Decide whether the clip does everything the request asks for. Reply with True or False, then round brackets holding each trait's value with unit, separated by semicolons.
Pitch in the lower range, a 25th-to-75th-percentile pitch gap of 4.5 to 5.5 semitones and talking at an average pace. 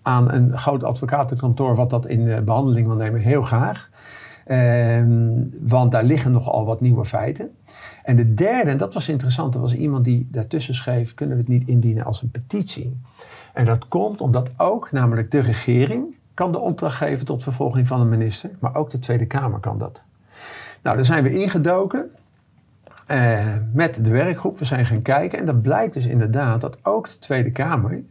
False (125 Hz; 3.0 semitones; 190 wpm)